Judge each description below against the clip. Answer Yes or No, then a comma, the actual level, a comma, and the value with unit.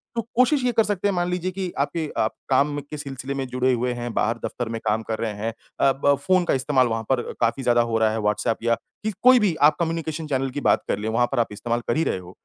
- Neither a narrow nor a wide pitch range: No, wide, 6.1 semitones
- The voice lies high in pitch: No, low, 135 Hz